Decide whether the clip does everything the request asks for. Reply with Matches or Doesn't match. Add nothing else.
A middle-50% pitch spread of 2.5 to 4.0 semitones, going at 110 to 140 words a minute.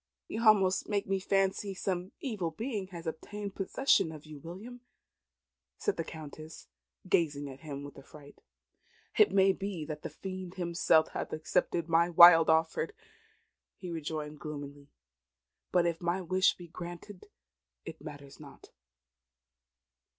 Matches